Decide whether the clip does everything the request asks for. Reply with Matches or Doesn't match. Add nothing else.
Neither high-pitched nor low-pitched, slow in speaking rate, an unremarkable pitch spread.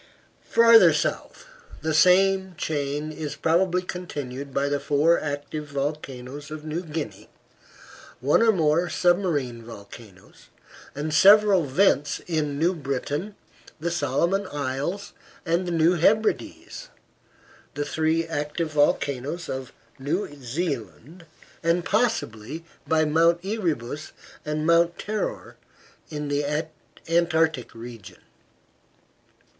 Matches